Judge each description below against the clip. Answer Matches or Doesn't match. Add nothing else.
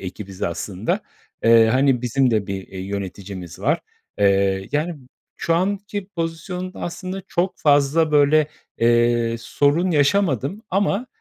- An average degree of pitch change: Doesn't match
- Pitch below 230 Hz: Matches